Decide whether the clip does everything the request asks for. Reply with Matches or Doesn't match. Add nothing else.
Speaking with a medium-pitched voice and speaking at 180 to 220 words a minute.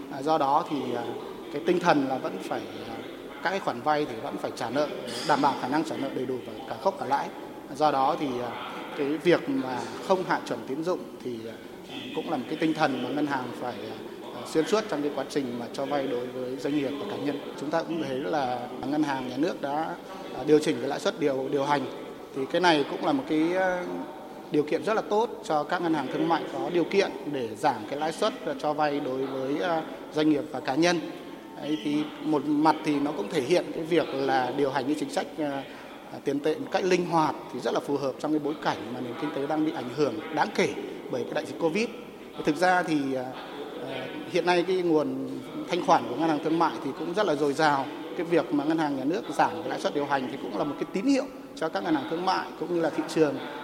Doesn't match